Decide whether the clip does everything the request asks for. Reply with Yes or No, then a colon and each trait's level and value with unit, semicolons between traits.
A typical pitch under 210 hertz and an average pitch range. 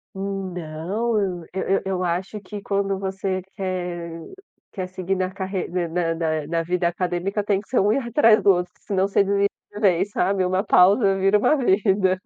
No: high, 190 Hz; narrow, 1.9 semitones